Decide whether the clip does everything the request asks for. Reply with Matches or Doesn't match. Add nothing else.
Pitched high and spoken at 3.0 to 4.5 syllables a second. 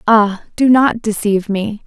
Matches